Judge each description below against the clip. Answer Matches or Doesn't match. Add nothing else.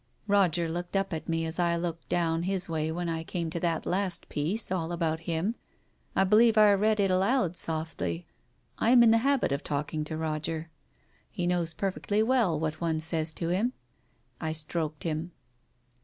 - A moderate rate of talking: Matches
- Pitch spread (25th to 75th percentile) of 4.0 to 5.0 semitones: Doesn't match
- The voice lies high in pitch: Doesn't match